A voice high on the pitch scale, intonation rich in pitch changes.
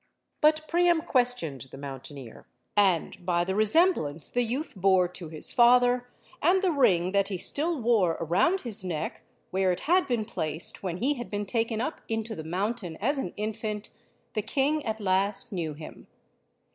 Yes: high, 210 Hz; wide, 5.9 semitones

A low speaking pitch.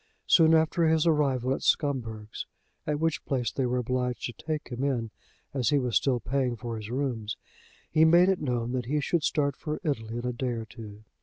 Yes: low, 130 Hz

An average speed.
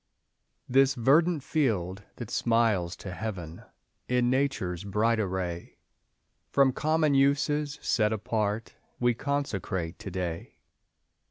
No: slow, 105 wpm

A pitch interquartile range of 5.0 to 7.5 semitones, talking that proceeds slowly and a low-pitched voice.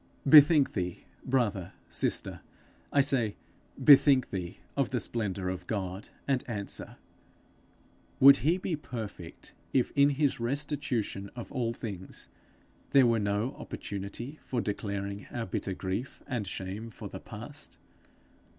Yes: average, 5.3 semitones; slow, 130 wpm; low, 115 Hz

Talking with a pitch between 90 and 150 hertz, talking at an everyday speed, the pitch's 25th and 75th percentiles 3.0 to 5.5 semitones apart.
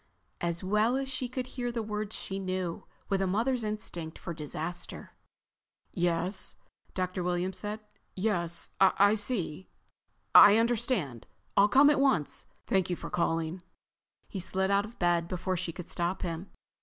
No: high, 190 Hz; average, 155 wpm; average, 3.7 semitones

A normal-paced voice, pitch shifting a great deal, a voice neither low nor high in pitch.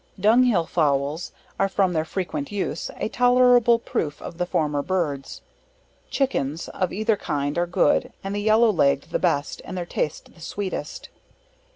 Yes: average, 160 wpm; wide, 6.2 semitones; medium, 180 Hz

